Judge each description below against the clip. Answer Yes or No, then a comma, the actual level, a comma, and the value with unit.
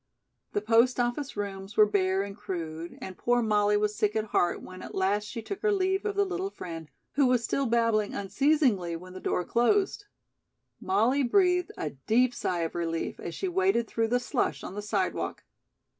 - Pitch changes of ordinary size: No, wide, 6.4 semitones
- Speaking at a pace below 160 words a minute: No, average, 190 wpm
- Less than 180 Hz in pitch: No, high, 220 Hz